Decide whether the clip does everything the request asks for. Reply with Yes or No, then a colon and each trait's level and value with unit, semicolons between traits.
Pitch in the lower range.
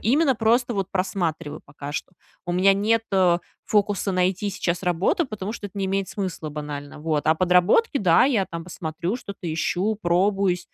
No: medium, 185 Hz